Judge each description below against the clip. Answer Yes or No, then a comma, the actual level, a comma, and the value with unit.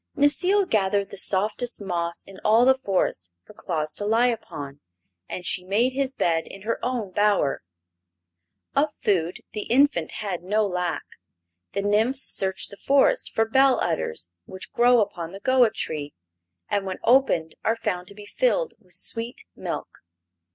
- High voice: Yes, high, 205 Hz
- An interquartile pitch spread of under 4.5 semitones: No, average, 5.3 semitones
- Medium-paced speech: Yes, average, 160 wpm